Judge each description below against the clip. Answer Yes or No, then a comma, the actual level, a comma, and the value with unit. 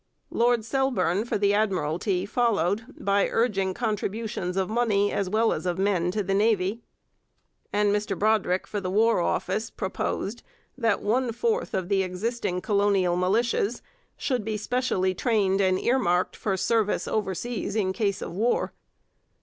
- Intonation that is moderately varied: Yes, average, 3.2 semitones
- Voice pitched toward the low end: No, high, 205 Hz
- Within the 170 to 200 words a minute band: No, average, 150 wpm